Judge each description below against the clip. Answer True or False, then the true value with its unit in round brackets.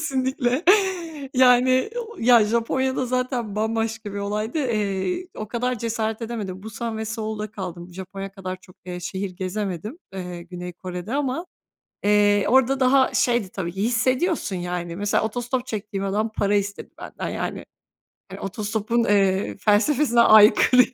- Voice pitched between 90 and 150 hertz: False (215 Hz)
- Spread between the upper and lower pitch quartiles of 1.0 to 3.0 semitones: False (4.2 semitones)